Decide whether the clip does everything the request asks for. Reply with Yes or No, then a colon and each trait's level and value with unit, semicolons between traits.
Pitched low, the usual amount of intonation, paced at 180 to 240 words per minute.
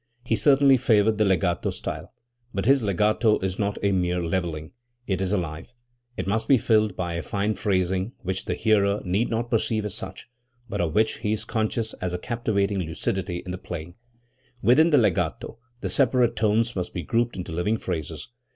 Yes: low, 100 Hz; average, 3.7 semitones; average, 190 wpm